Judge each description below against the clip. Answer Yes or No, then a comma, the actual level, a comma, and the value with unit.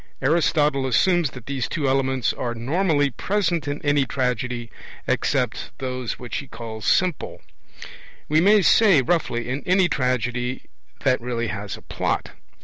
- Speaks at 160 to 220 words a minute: No, average, 140 wpm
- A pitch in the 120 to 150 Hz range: Yes, low, 135 Hz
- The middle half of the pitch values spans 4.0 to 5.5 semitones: Yes, average, 4.4 semitones